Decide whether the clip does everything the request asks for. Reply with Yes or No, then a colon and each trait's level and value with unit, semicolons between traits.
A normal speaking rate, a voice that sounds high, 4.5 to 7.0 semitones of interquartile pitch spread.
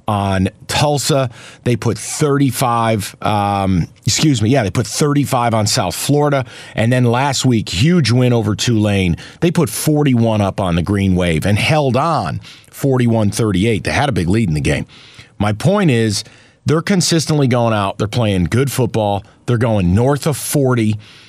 No: average, 170 wpm; low, 120 Hz; average, 4.9 semitones